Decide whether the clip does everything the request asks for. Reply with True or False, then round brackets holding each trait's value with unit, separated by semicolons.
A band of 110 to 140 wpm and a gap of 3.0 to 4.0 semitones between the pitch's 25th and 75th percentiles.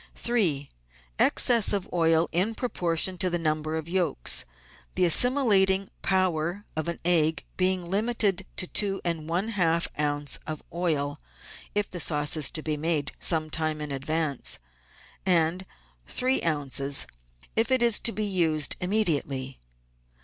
True (135 wpm; 3.7 semitones)